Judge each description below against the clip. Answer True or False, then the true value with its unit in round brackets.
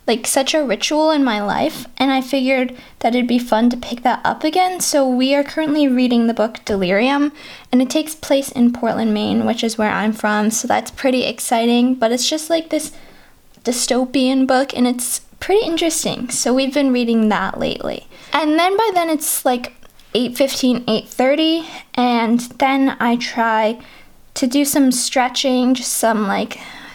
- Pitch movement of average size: True (3.4 semitones)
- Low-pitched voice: False (255 Hz)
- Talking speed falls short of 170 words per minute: False (175 wpm)